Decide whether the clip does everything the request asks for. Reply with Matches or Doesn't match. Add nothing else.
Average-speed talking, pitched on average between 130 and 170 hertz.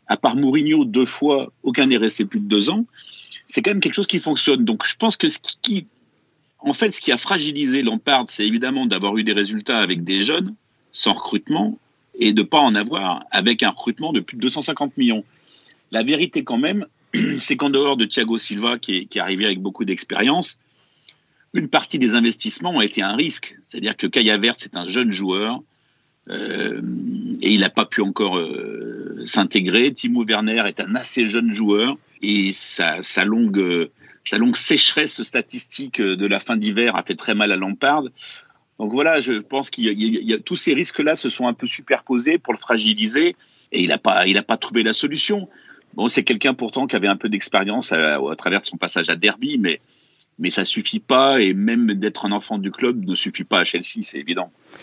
Matches